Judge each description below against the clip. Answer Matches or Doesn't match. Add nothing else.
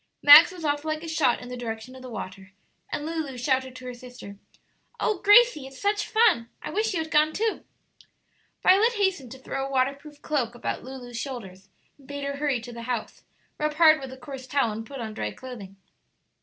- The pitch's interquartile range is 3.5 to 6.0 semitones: Matches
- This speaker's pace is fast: Matches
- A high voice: Matches